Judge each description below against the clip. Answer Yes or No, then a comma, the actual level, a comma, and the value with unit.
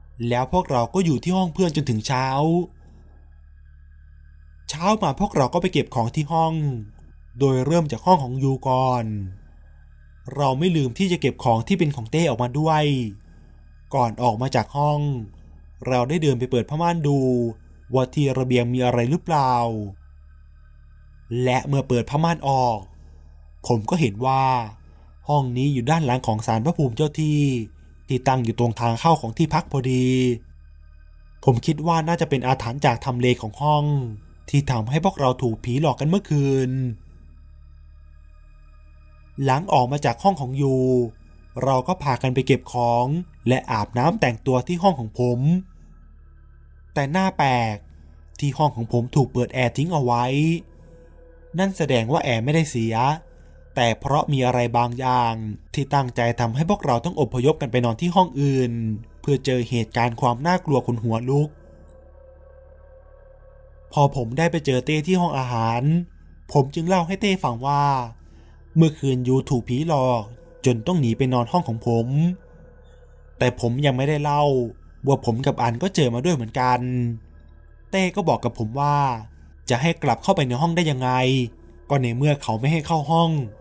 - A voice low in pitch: Yes, low, 125 Hz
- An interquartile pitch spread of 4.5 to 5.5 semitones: Yes, average, 5.2 semitones